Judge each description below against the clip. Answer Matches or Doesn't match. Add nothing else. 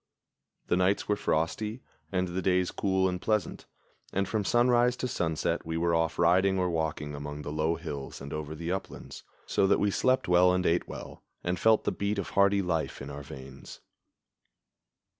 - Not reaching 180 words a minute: Doesn't match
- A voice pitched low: Matches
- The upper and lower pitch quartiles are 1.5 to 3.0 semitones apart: Doesn't match